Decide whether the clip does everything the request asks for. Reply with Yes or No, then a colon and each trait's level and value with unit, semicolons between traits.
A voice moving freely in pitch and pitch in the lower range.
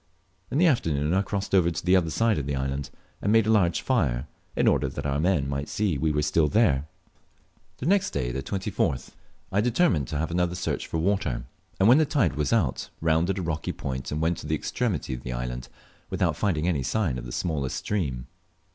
Yes: wide, 6.2 semitones; very low, 80 Hz